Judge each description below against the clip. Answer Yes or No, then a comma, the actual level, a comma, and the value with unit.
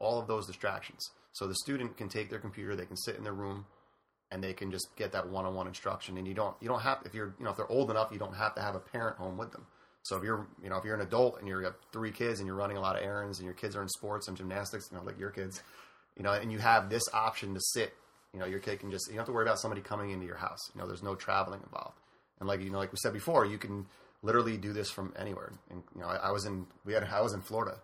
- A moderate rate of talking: No, fast, 310 wpm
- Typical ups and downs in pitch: No, narrow, 2.3 semitones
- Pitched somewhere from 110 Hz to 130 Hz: No, low, 100 Hz